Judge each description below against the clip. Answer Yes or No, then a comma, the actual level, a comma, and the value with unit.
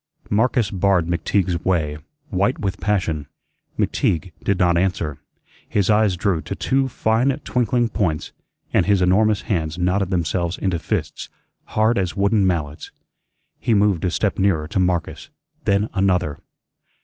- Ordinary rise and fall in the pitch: Yes, average, 3.4 semitones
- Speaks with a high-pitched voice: No, very low, 95 Hz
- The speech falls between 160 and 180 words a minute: No, average, 140 wpm